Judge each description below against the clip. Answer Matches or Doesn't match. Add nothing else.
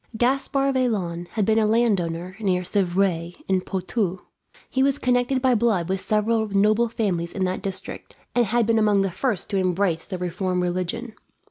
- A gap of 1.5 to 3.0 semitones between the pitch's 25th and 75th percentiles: Doesn't match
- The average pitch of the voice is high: Matches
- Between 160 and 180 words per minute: Matches